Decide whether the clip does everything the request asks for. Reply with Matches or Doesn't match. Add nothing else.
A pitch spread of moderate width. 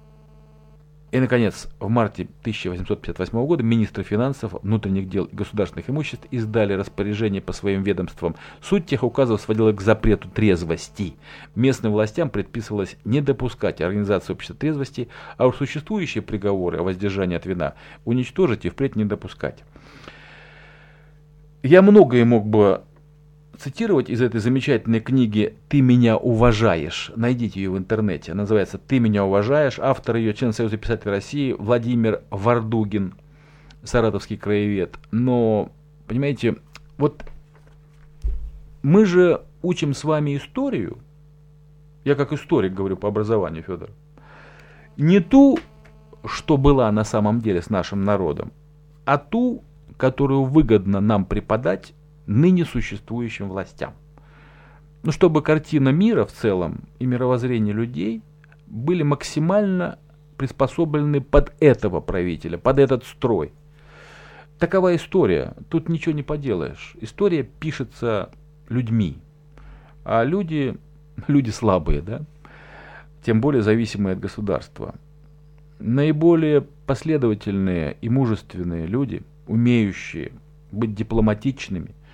Doesn't match